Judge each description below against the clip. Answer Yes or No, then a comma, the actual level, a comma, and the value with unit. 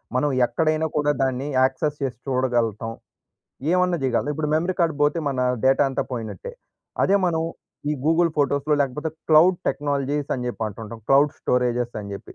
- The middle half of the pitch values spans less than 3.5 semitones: No, average, 3.8 semitones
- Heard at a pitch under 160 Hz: Yes, medium, 140 Hz